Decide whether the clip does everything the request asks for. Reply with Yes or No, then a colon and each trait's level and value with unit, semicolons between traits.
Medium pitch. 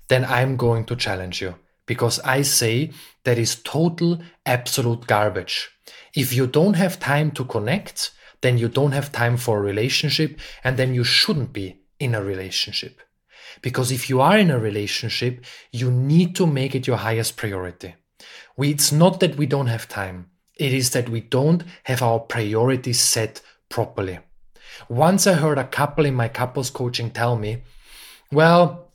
No: low, 125 Hz